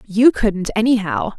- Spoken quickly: No, slow, 130 wpm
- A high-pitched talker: Yes, high, 220 Hz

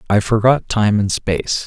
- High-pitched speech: No, low, 110 Hz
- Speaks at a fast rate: No, average, 180 wpm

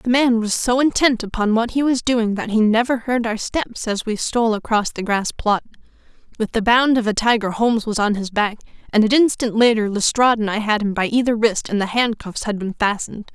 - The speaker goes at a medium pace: No, fast, 235 wpm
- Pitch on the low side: No, high, 225 Hz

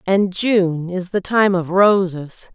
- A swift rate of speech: No, average, 165 wpm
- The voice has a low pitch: No, medium, 185 Hz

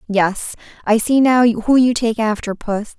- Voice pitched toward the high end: Yes, high, 225 Hz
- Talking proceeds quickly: No, average, 180 wpm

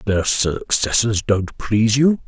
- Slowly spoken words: Yes, slow, 130 wpm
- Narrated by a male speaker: Yes, male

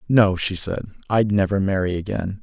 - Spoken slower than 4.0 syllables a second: No, 5.0 syllables/s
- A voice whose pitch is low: Yes, low, 100 Hz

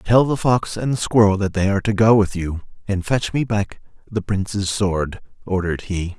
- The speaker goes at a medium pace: No, fast, 215 wpm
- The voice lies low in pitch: Yes, low, 100 Hz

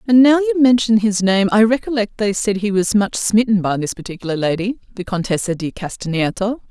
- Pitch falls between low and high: No, high, 205 Hz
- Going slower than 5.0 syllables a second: No, 5.6 syllables/s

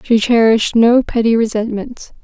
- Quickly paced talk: No, slow, 135 wpm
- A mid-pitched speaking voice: No, high, 230 Hz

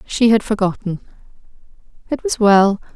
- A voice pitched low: No, high, 210 Hz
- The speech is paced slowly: Yes, slow, 120 wpm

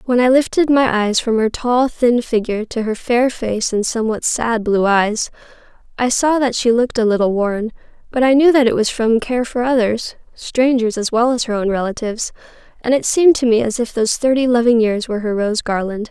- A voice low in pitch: No, high, 235 Hz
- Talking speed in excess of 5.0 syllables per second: Yes, 5.4 syllables/s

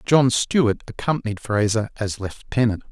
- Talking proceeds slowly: Yes, slow, 125 wpm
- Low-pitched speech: Yes, low, 115 Hz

